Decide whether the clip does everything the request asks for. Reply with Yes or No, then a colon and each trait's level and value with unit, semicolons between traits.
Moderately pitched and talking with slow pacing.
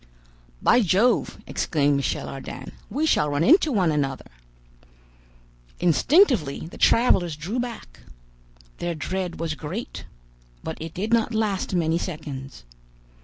Yes: medium, 175 Hz; slow, 120 wpm